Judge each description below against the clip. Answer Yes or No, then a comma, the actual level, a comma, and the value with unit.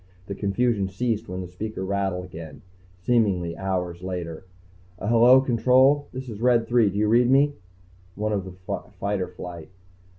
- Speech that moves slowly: No, average, 160 wpm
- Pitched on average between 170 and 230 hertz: No, low, 100 Hz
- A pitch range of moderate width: Yes, average, 4.6 semitones